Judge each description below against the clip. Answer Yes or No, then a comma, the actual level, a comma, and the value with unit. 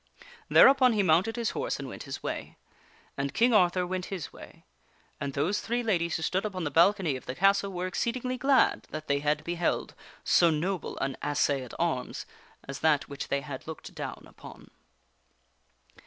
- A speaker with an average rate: Yes, average, 180 wpm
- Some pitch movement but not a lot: No, wide, 5.9 semitones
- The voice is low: No, medium, 175 Hz